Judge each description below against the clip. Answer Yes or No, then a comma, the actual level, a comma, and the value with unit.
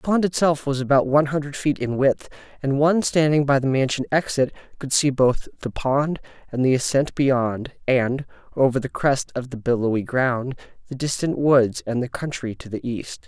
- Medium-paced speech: Yes, average, 195 wpm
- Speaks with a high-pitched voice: No, low, 135 Hz